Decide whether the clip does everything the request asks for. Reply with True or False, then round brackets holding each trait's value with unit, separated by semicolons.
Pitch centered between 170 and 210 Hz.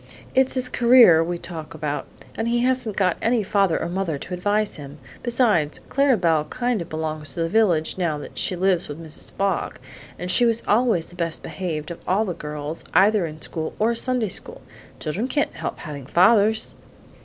True (185 Hz)